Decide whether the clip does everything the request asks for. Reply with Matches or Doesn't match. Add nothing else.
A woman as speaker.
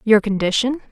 Matches